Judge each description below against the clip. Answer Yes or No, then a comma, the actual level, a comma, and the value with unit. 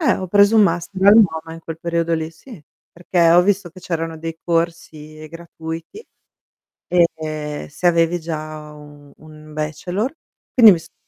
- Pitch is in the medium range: Yes, medium, 165 Hz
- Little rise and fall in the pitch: Yes, narrow, 2.2 semitones